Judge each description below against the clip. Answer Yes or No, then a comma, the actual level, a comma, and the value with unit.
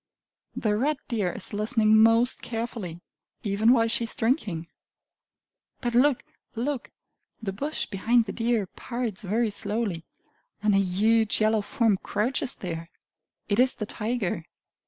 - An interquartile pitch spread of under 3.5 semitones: Yes, average, 2.9 semitones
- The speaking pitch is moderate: No, high, 220 Hz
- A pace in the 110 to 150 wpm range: Yes, slow, 135 wpm